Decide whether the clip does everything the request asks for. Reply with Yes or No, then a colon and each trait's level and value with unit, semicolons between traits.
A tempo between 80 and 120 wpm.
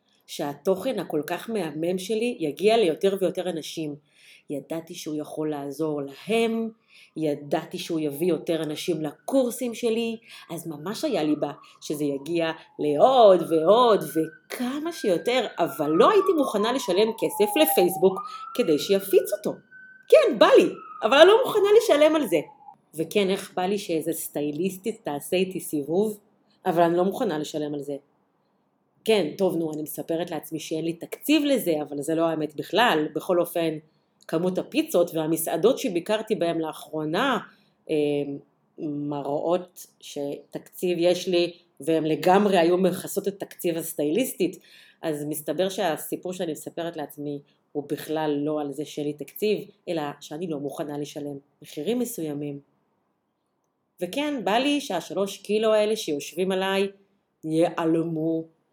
No: average, 135 wpm